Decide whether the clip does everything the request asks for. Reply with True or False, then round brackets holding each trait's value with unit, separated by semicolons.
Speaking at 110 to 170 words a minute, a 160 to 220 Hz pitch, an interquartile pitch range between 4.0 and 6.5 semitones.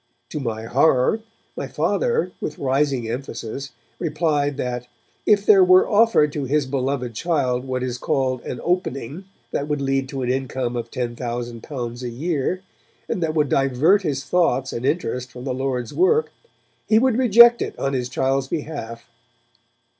False (160 wpm; 135 Hz; 4.5 semitones)